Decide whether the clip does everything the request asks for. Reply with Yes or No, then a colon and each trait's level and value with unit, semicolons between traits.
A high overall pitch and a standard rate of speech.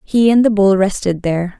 No: high, 200 Hz; fast, 225 wpm